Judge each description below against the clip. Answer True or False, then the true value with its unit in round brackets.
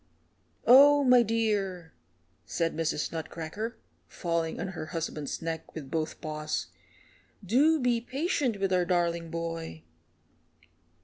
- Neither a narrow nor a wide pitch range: False (6.1 semitones)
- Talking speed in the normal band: False (115 wpm)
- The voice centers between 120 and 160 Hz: False (175 Hz)